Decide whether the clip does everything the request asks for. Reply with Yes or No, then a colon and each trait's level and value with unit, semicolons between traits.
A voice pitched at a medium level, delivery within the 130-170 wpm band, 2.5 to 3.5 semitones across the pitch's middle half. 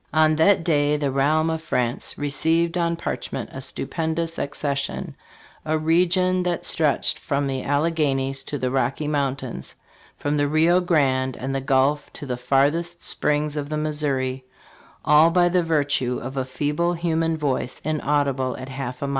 Yes: medium, 145 Hz; average, 165 wpm; average, 3.1 semitones